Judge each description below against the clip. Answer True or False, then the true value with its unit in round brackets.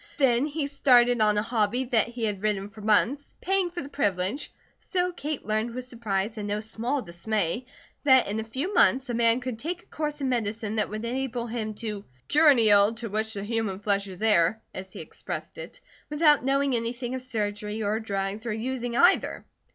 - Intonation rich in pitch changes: False (3.8 semitones)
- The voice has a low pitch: False (230 Hz)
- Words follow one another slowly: False (205 wpm)